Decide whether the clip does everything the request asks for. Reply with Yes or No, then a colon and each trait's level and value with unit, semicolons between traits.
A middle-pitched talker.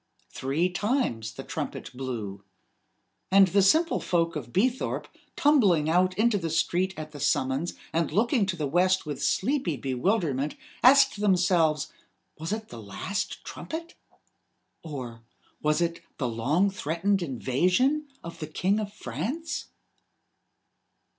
Yes: medium, 175 Hz